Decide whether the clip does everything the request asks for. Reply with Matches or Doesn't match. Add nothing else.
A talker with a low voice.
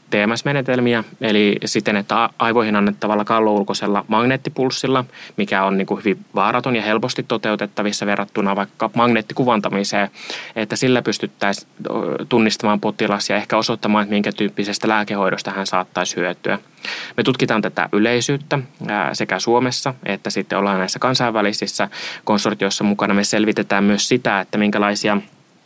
Matches